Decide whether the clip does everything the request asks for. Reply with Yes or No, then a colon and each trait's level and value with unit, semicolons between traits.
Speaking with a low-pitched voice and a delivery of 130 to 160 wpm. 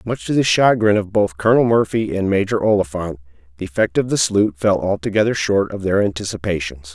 No: low, 100 Hz; average, 190 wpm